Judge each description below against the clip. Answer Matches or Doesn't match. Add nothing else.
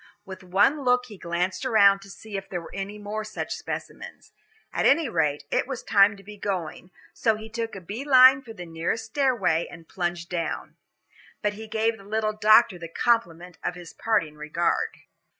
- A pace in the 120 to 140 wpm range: Doesn't match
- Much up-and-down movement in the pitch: Doesn't match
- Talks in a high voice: Matches